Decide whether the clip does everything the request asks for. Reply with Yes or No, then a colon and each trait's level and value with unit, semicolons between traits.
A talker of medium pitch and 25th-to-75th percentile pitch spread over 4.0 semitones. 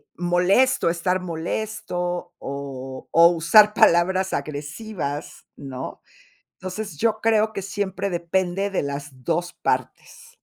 Yes: medium, 175 Hz; average, 4.6 semitones